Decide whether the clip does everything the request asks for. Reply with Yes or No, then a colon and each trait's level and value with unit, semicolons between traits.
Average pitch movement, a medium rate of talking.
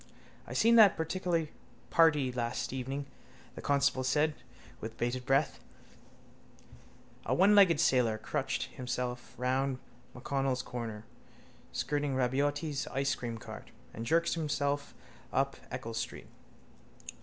No: average, 3.3 semitones; slow, 110 wpm